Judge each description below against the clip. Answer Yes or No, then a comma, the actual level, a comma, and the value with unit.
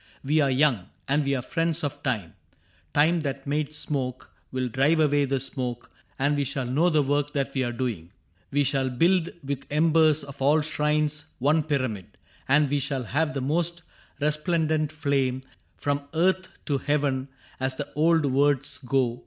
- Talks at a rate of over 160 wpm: Yes, average, 170 wpm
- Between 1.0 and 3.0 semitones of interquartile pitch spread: Yes, narrow, 2.4 semitones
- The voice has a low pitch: No, medium, 145 Hz